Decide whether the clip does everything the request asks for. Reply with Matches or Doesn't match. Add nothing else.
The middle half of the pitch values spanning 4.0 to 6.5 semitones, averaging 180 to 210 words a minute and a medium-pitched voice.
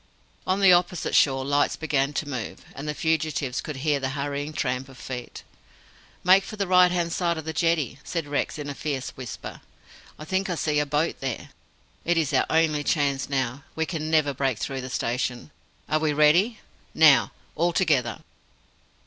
Doesn't match